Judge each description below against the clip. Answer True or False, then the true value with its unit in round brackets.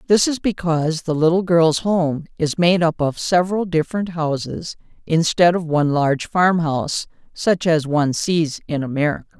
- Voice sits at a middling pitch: True (165 Hz)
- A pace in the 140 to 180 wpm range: True (160 wpm)